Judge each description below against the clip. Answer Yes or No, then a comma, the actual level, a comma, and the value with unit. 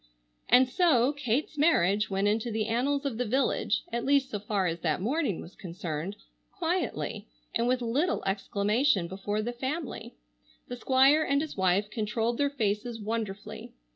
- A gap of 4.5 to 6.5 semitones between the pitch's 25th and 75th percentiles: Yes, average, 4.8 semitones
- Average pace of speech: Yes, average, 160 wpm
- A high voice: Yes, high, 230 Hz